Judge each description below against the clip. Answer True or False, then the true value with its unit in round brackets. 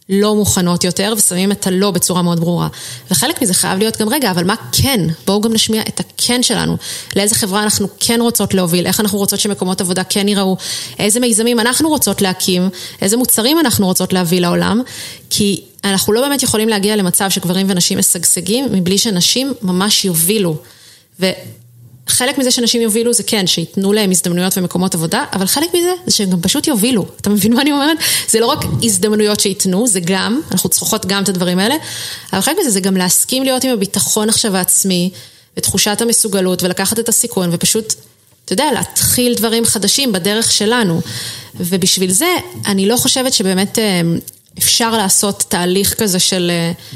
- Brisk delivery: True (175 wpm)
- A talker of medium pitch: False (200 Hz)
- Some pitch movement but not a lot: True (3.5 semitones)